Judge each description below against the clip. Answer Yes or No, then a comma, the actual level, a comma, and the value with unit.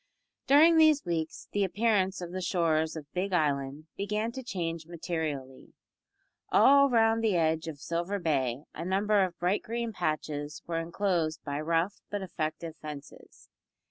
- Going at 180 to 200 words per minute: No, average, 150 wpm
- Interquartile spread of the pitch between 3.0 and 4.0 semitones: No, average, 4.6 semitones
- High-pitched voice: No, medium, 170 Hz